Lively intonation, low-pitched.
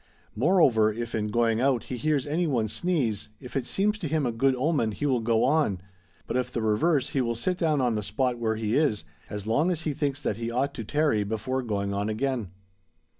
No: average, 4.8 semitones; low, 125 Hz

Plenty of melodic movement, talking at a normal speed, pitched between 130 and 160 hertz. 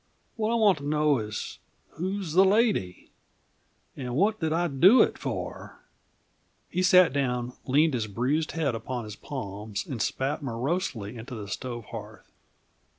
Yes: wide, 7.1 semitones; average, 150 wpm; medium, 140 Hz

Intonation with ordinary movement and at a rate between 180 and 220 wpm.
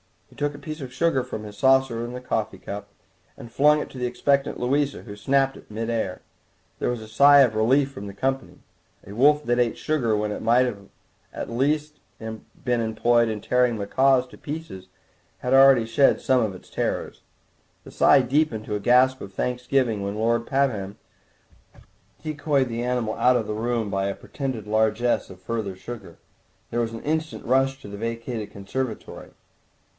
Yes: average, 3.6 semitones; average, 190 wpm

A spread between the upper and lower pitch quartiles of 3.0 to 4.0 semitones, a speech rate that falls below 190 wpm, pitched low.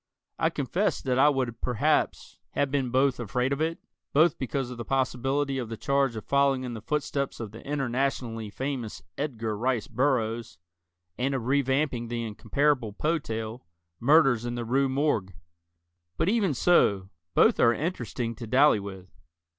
Yes: average, 3.4 semitones; average, 160 wpm; low, 130 Hz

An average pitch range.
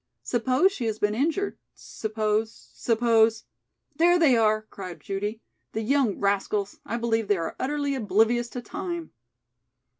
Yes: average, 3.8 semitones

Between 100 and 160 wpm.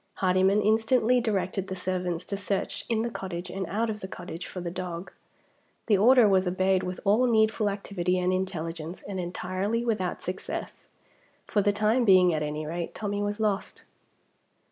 No: average, 170 wpm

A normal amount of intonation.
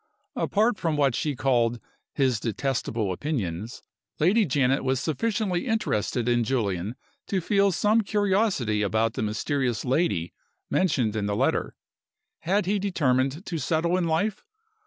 No: wide, 8.1 semitones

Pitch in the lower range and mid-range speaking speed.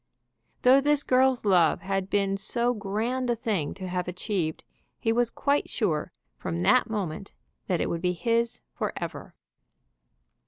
No: high, 205 Hz; average, 150 wpm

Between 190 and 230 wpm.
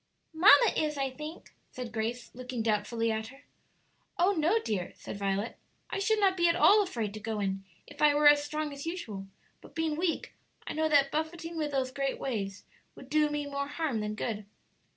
Yes: average, 200 wpm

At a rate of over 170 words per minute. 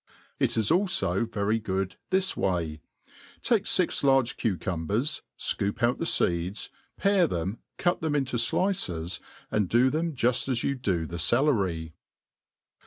No: average, 140 wpm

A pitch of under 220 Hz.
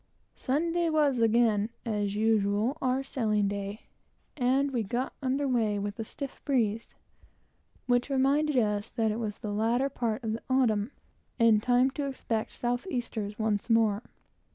No: high, 230 Hz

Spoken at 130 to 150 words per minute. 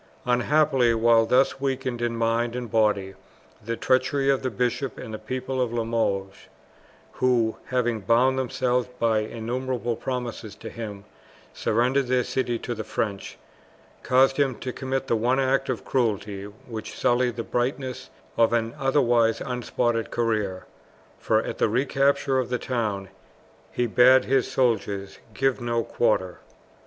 Yes: average, 145 wpm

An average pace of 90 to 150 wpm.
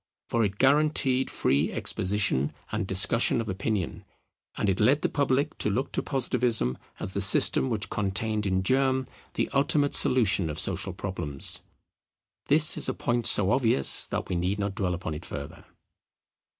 No: average, 165 wpm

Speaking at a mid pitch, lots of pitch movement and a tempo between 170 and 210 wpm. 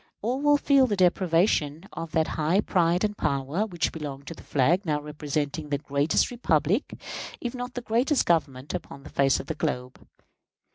Yes: medium, 165 Hz; wide, 6.4 semitones; average, 180 wpm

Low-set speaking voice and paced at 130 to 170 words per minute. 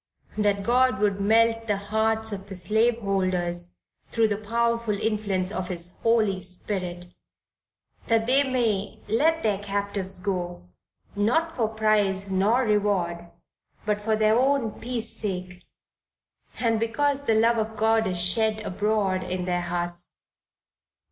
No: high, 210 Hz; slow, 135 wpm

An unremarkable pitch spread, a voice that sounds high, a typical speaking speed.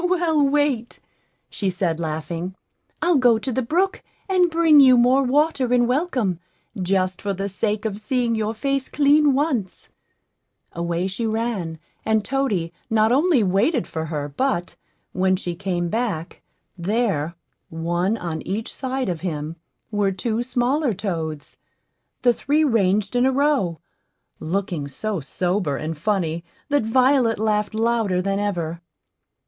No: wide, 6.4 semitones; high, 215 Hz; average, 145 wpm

